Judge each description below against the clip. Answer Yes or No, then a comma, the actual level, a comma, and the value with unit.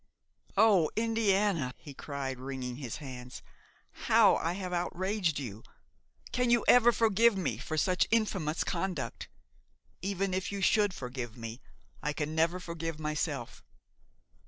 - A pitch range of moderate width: No, wide, 6.3 semitones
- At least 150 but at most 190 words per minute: No, slow, 135 wpm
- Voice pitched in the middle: Yes, medium, 170 Hz